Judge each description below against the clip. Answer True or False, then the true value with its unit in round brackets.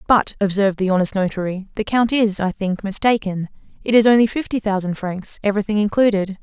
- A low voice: False (205 Hz)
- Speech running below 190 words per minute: True (175 wpm)